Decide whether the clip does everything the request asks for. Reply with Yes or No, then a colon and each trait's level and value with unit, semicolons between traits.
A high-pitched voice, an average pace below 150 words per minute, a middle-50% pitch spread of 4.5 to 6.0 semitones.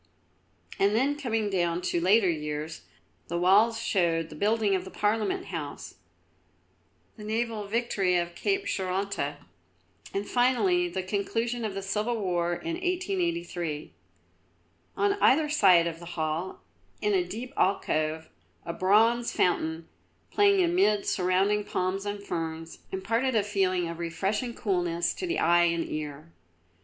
Yes: high, 195 Hz; average, 140 wpm; average, 5.2 semitones